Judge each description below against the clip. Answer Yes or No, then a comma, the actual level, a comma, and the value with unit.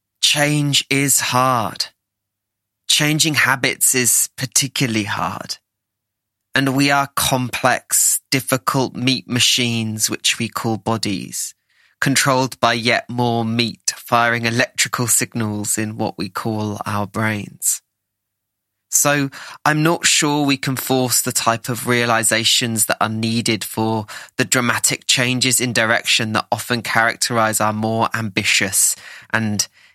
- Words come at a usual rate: No, slow, 120 wpm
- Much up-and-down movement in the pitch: No, average, 3.2 semitones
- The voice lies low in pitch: Yes, low, 115 Hz